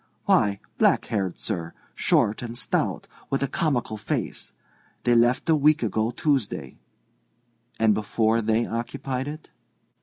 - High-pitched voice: No, low, 115 Hz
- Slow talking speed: Yes, slow, 130 wpm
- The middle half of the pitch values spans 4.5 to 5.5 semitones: No, average, 4.0 semitones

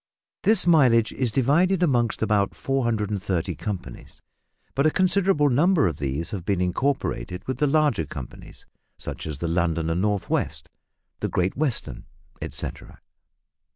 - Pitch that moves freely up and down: Yes, wide, 8.7 semitones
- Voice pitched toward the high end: No, low, 110 Hz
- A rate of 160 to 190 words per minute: No, average, 140 wpm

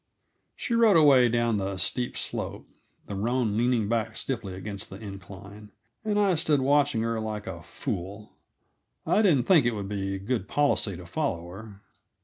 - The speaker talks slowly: No, average, 165 wpm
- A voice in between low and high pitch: No, low, 110 Hz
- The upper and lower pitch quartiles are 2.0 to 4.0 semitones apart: No, average, 5.1 semitones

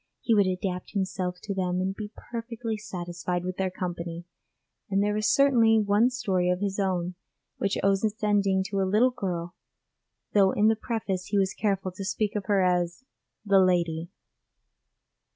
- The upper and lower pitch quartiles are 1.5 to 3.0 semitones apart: Yes, narrow, 2.6 semitones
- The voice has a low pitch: No, high, 195 Hz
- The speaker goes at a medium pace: Yes, average, 170 wpm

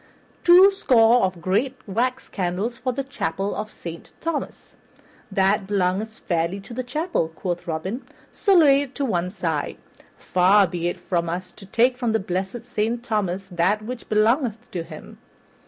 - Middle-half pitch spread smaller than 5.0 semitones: No, average, 5.3 semitones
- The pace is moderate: Yes, average, 160 wpm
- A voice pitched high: Yes, high, 210 Hz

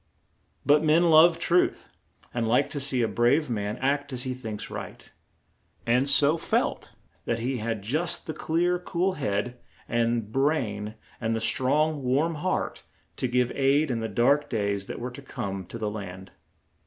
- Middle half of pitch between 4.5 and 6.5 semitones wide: Yes, average, 4.8 semitones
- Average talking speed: Yes, average, 170 wpm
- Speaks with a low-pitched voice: Yes, low, 125 Hz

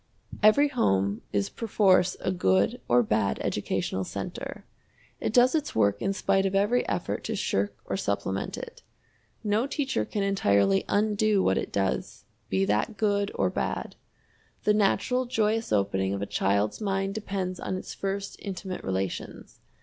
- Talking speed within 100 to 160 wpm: Yes, average, 155 wpm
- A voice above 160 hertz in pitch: Yes, high, 190 Hz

